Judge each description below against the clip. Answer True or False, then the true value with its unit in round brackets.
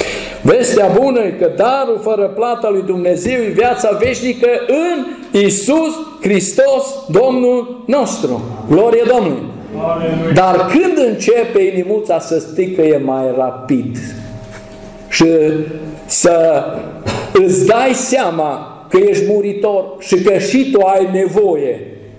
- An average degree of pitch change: False (7.8 semitones)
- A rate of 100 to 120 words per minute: True (115 wpm)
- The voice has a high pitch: True (205 Hz)